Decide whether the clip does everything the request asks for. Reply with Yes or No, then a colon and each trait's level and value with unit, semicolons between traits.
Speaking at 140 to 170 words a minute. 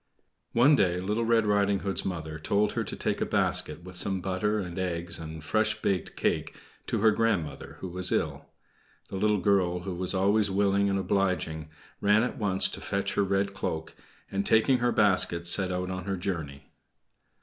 No: average, 185 wpm